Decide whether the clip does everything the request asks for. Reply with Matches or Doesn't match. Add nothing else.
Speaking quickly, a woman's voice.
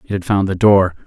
Doesn't match